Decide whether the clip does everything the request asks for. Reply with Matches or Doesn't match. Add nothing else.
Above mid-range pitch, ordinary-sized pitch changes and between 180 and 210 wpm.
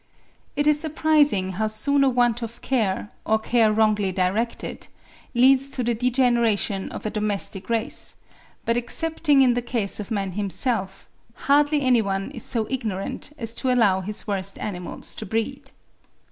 Doesn't match